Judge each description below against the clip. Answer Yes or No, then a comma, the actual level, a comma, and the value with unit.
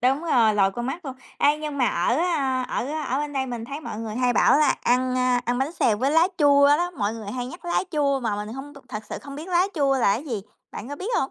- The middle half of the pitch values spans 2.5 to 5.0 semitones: Yes, average, 3.6 semitones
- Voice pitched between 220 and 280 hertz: Yes, very high, 270 Hz